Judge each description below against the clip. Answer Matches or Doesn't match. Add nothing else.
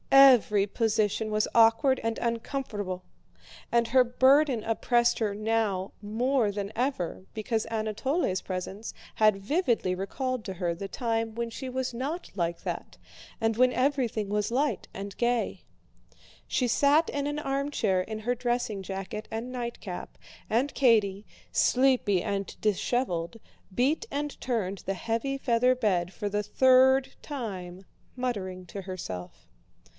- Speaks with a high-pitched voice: Matches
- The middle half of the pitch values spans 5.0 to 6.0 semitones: Doesn't match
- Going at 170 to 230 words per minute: Doesn't match